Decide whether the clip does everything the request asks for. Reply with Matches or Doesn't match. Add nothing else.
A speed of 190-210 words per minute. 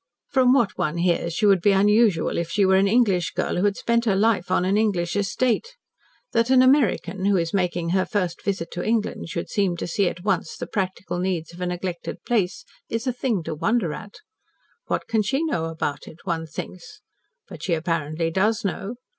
Matches